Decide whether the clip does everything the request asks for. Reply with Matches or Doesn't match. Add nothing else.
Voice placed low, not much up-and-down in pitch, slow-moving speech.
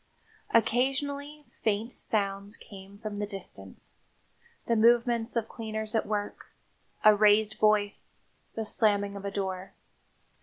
Doesn't match